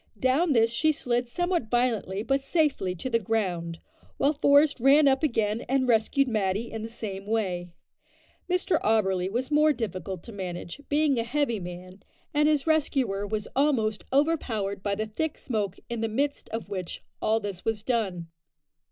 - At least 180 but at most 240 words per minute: No, average, 170 wpm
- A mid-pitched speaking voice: No, high, 225 Hz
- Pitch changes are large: Yes, wide, 5.7 semitones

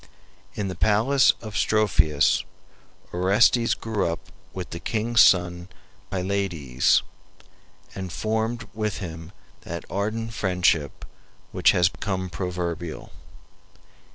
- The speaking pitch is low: Yes, very low, 95 Hz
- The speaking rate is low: Yes, slow, 100 wpm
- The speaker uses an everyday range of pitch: Yes, average, 3.8 semitones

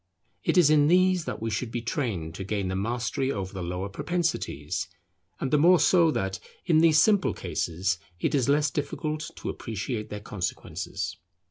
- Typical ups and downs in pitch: No, wide, 7.9 semitones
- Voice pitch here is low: Yes, low, 125 Hz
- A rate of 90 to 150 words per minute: No, average, 175 wpm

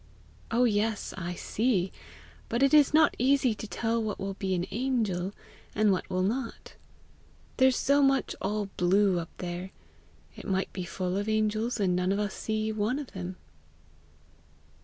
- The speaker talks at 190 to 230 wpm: No, average, 165 wpm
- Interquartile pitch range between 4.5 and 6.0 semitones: No, average, 4.0 semitones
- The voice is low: No, high, 210 Hz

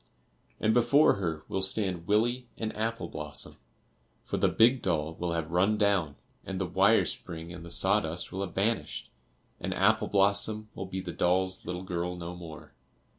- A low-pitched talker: Yes, very low, 95 Hz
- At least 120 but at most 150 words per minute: No, average, 175 wpm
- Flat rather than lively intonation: No, average, 3.7 semitones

